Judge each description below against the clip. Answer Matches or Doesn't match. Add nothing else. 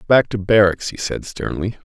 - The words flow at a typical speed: Matches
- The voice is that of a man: Matches